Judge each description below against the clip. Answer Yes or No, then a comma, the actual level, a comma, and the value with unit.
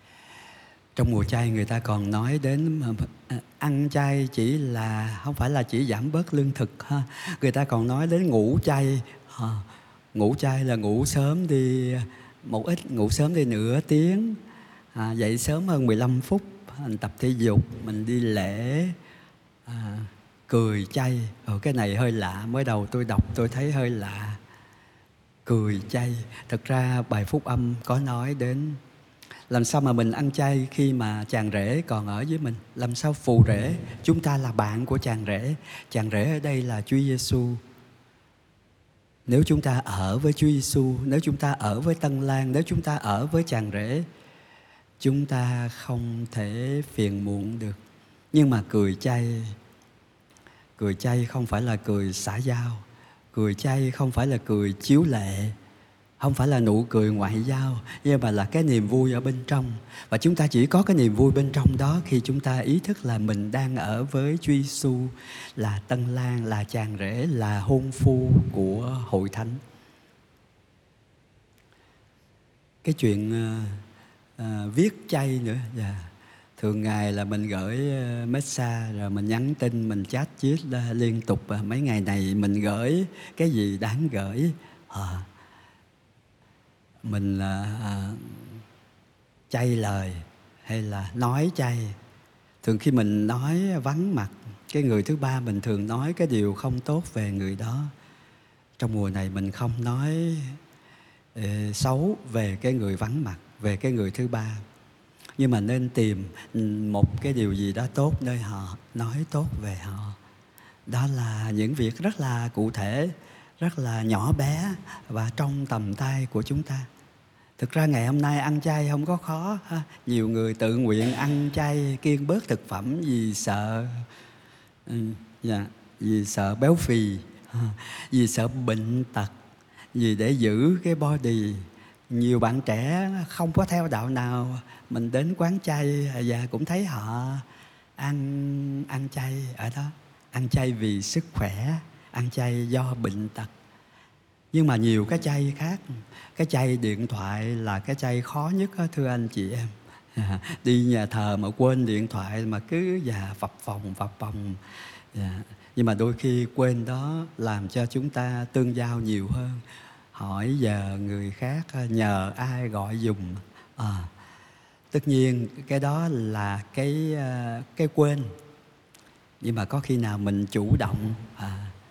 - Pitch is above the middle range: No, low, 120 Hz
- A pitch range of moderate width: Yes, average, 4.4 semitones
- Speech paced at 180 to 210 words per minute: No, slow, 165 wpm